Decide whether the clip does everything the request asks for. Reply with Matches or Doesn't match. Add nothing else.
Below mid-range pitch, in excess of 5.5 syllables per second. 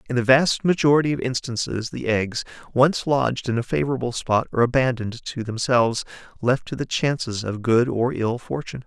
Matches